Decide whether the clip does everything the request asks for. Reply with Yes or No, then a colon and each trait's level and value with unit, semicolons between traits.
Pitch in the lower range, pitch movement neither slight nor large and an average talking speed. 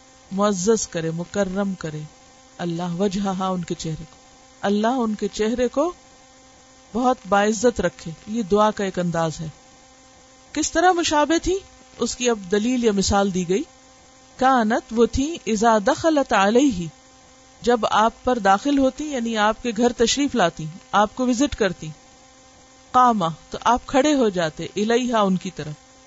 No: high, 235 Hz; average, 4.9 semitones; average, 130 wpm